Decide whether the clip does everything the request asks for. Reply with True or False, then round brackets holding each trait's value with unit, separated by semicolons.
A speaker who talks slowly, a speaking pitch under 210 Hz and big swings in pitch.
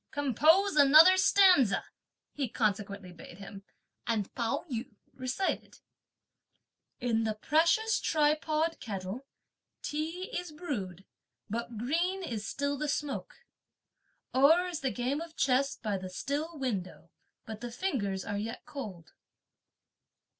False (120 wpm; 265 Hz; 6.7 semitones)